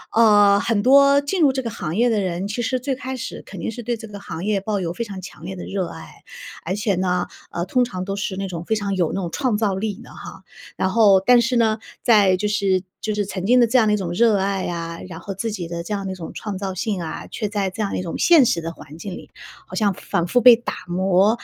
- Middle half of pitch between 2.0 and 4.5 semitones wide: Yes, average, 3.6 semitones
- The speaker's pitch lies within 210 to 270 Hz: No, high, 200 Hz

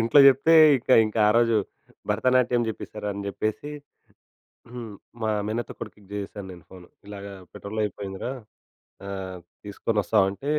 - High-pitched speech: No, low, 105 Hz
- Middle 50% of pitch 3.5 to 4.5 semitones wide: No, average, 2.8 semitones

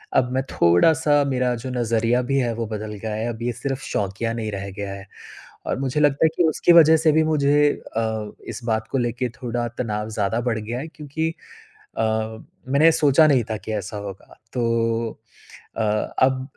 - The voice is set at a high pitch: No, low, 120 Hz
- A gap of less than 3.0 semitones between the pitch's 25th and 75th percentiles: No, average, 4.3 semitones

